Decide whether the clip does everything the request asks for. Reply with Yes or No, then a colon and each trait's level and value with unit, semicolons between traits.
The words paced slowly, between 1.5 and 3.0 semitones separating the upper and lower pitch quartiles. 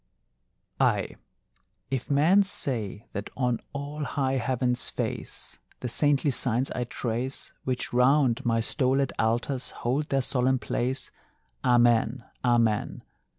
Yes: slow, 115 wpm; narrow, 2.4 semitones